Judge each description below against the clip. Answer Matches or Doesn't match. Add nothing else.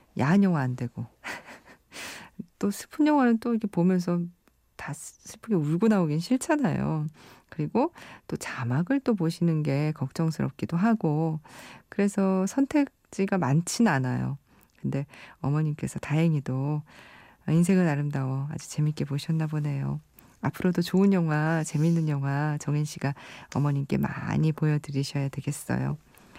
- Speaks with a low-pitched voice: Doesn't match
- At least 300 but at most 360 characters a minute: Doesn't match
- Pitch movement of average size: Matches